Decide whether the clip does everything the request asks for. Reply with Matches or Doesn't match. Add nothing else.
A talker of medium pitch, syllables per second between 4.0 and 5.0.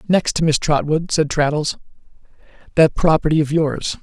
Matches